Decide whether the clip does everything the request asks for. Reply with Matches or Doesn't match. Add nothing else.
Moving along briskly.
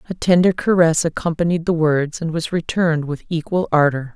Doesn't match